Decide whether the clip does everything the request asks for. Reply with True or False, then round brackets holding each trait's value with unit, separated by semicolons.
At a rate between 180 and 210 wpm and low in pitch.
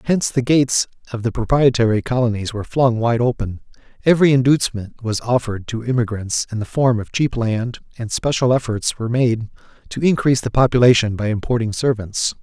False (170 wpm; 120 Hz)